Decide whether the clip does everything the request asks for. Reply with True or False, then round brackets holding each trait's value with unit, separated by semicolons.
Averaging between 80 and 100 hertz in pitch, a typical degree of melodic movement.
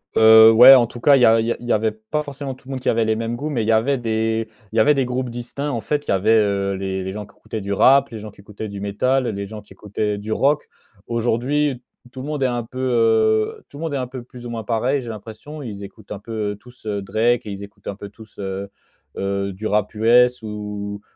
False (110 Hz; 3.4 semitones)